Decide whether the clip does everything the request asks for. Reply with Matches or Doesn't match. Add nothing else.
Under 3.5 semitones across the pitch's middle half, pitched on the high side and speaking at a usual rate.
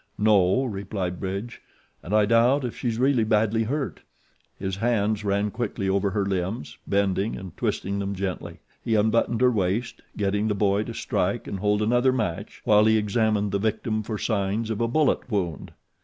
Doesn't match